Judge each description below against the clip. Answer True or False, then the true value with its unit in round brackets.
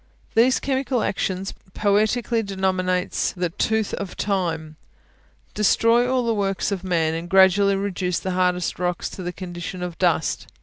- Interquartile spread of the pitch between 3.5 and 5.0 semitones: False (2.8 semitones)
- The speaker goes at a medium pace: True (145 wpm)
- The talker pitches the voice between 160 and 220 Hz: True (190 Hz)